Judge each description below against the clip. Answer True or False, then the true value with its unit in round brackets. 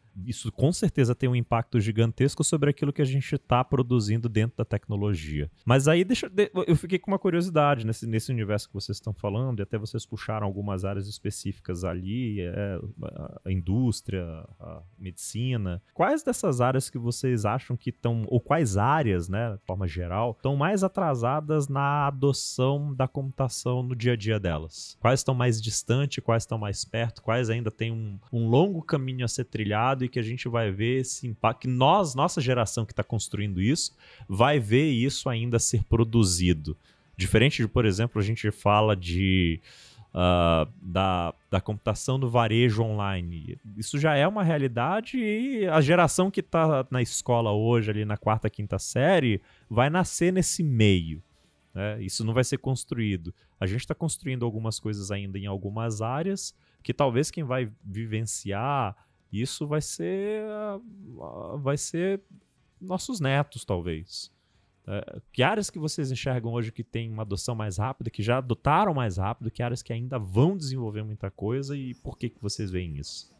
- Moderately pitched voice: False (120 Hz)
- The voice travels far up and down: False (4.8 semitones)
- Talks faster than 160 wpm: True (170 wpm)